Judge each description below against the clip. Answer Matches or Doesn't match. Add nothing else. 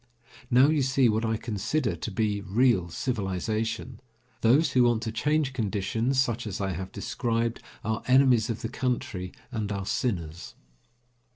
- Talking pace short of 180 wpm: Matches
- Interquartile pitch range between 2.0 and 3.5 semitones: Doesn't match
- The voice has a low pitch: Matches